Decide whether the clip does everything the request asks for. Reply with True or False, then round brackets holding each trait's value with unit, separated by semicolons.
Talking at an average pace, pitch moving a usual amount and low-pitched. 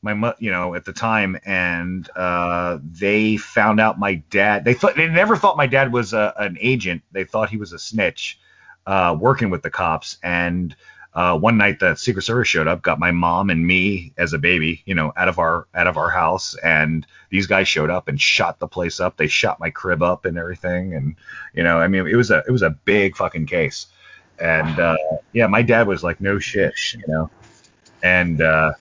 False (220 wpm; 4.4 semitones; 95 Hz)